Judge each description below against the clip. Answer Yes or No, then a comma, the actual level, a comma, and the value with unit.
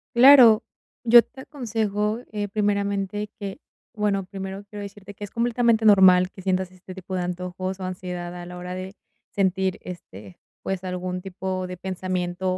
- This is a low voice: No, high, 190 Hz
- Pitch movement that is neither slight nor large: No, narrow, 2.2 semitones